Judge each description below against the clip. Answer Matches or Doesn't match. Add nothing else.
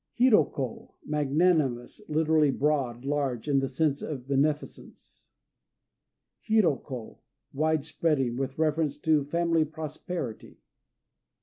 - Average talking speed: Doesn't match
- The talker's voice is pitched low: Doesn't match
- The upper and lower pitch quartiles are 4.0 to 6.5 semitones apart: Doesn't match